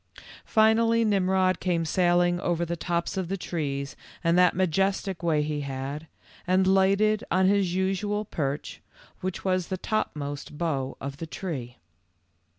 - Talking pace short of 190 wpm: Yes, average, 150 wpm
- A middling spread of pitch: Yes, average, 3.8 semitones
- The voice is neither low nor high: Yes, medium, 180 Hz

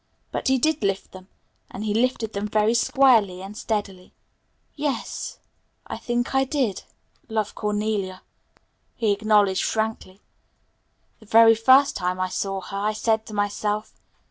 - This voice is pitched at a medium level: No, high, 215 Hz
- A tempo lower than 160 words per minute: Yes, average, 145 wpm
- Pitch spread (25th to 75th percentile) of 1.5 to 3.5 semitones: Yes, narrow, 2.5 semitones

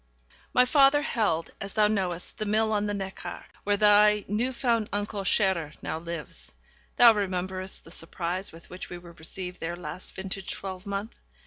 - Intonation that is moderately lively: Yes, average, 3.0 semitones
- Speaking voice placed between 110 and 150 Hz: No, high, 195 Hz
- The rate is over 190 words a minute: No, average, 165 wpm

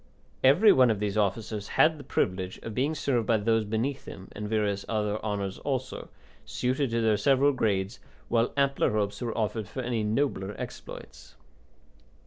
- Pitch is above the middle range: No, low, 110 Hz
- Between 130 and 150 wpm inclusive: No, average, 165 wpm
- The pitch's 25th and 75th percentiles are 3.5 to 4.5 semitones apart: Yes, average, 3.9 semitones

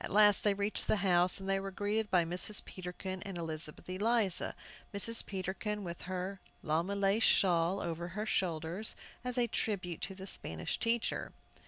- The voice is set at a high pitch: Yes, high, 195 Hz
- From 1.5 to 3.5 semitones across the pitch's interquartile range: Yes, average, 2.7 semitones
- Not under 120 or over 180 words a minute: Yes, average, 165 wpm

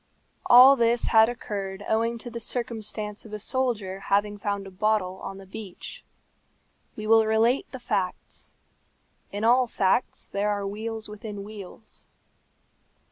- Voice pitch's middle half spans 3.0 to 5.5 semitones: No, narrow, 2.4 semitones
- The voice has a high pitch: Yes, high, 215 Hz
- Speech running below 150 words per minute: Yes, average, 140 wpm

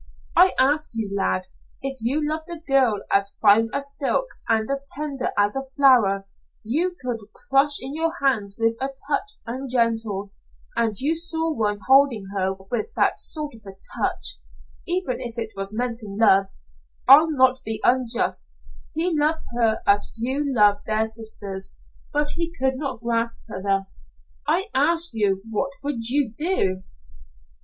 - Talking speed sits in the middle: Yes, average, 160 wpm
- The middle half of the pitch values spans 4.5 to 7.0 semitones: Yes, average, 5.2 semitones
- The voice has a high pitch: Yes, high, 245 Hz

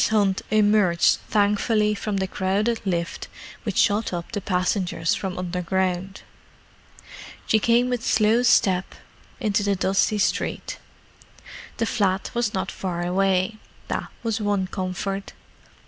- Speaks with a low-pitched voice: No, high, 195 Hz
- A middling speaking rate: No, slow, 125 wpm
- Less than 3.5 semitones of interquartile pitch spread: Yes, narrow, 2.4 semitones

